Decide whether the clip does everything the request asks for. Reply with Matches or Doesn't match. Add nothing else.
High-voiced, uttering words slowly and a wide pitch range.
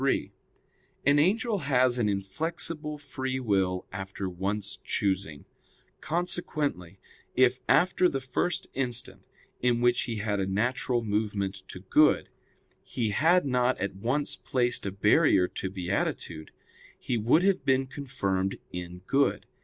Doesn't match